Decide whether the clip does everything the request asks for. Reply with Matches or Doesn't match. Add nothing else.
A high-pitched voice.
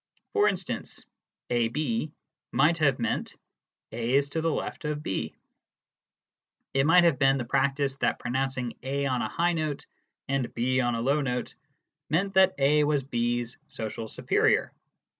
Doesn't match